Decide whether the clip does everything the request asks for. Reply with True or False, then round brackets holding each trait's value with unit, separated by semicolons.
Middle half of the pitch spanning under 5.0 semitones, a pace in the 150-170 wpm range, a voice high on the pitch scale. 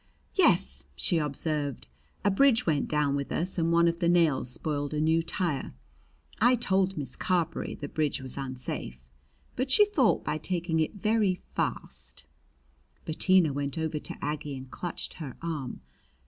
False (4.2 semitones; 160 wpm; 160 Hz)